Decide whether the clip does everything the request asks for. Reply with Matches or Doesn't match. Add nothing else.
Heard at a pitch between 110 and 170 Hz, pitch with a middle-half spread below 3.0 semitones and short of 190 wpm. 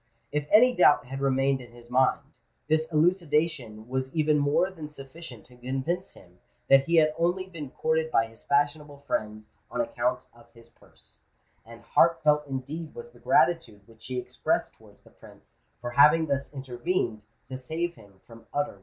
Doesn't match